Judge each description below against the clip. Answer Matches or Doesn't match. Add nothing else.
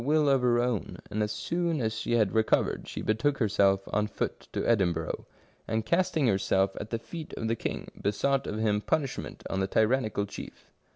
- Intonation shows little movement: Doesn't match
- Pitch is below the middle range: Matches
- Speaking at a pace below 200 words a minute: Matches